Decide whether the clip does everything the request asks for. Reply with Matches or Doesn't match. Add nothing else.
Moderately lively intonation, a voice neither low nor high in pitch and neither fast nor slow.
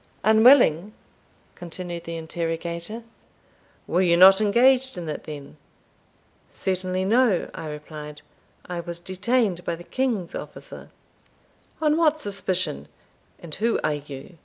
Doesn't match